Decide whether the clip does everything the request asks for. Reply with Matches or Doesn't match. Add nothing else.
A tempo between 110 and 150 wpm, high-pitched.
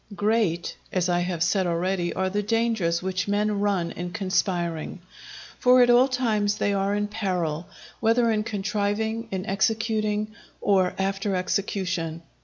Matches